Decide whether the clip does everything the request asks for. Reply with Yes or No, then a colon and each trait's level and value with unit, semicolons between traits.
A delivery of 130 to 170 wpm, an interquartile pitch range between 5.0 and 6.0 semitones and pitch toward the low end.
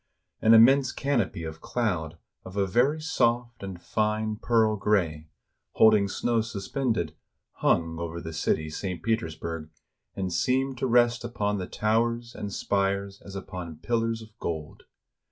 Yes: average, 140 wpm; average, 5.3 semitones; low, 105 Hz